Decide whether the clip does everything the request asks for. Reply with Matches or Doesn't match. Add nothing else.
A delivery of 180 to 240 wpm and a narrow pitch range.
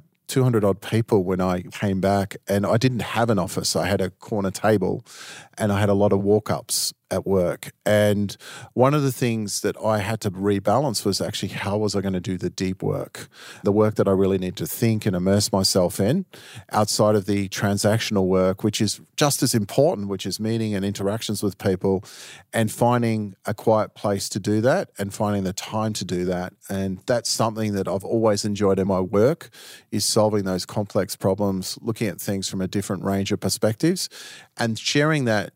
Matches